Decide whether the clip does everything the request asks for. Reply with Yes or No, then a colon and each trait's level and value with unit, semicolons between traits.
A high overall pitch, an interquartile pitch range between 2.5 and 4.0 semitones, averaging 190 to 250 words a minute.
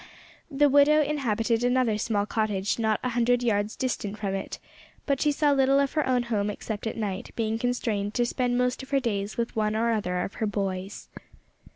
Yes: high, 230 Hz; average, 3.6 semitones; average, 200 wpm